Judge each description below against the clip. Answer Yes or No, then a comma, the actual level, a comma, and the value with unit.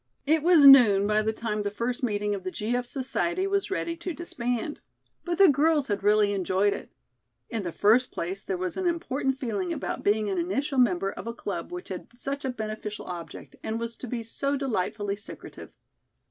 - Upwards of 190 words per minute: Yes, average, 200 wpm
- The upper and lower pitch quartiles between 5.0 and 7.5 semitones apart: Yes, wide, 5.4 semitones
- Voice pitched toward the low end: No, high, 225 Hz